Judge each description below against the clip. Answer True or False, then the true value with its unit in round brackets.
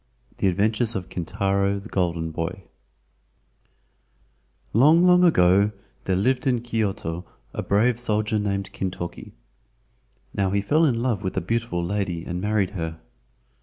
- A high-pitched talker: False (100 Hz)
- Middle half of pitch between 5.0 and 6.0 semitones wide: False (4.0 semitones)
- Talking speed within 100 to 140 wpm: True (135 wpm)